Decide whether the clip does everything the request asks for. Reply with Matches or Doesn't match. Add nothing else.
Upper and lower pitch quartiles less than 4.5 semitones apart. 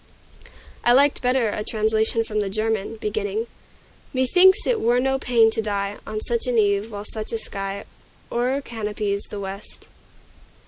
Matches